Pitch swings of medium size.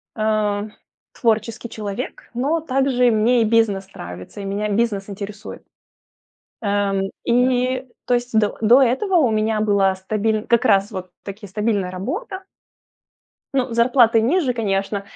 Yes: average, 3.4 semitones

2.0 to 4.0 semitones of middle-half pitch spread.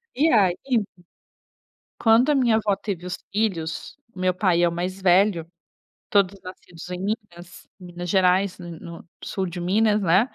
Yes: average, 3.1 semitones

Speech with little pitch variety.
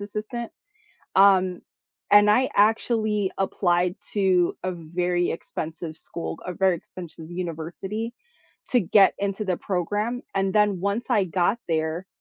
No: average, 3.0 semitones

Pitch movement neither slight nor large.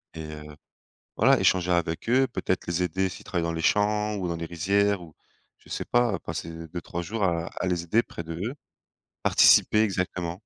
Yes: average, 3.5 semitones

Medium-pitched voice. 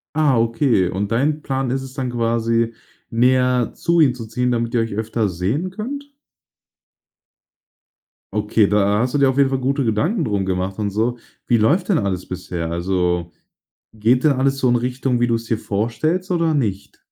No: low, 120 Hz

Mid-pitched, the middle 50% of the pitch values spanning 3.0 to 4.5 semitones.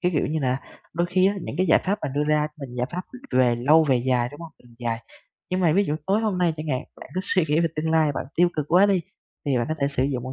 No: medium, 155 Hz; average, 5.3 semitones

